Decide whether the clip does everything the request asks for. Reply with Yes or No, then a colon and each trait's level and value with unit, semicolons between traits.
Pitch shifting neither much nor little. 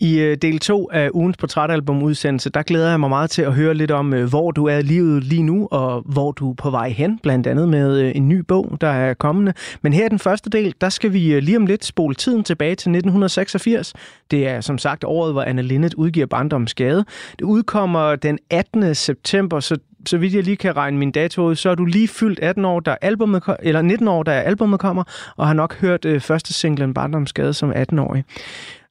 Yes: average, 4.4 semitones